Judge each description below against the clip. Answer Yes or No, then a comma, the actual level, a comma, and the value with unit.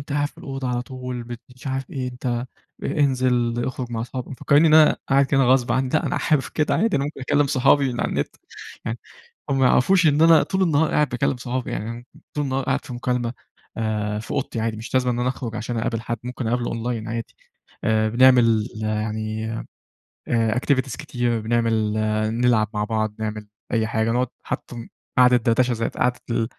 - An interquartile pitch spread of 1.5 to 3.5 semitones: Yes, average, 2.7 semitones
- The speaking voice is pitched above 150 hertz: No, low, 125 Hz